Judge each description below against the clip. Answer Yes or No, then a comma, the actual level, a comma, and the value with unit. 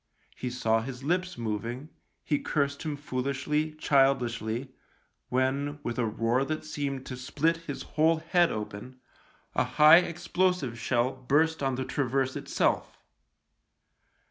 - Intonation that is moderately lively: Yes, average, 3.7 semitones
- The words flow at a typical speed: No, slow, 130 wpm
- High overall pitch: No, low, 135 Hz